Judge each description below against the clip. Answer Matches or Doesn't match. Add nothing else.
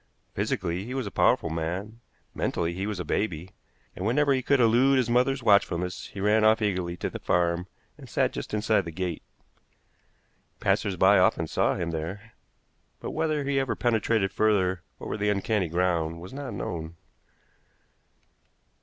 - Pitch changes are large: Doesn't match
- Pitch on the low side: Matches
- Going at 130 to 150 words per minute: Doesn't match